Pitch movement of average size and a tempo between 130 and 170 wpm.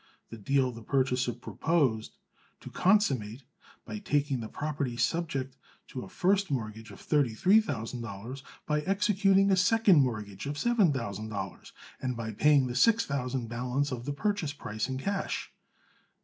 No: wide, 6.7 semitones; average, 160 wpm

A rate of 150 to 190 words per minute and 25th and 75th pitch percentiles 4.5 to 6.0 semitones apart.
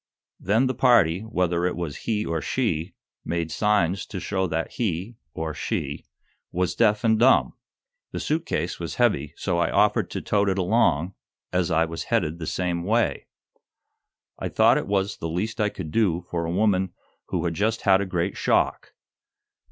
No: average, 180 wpm; average, 4.1 semitones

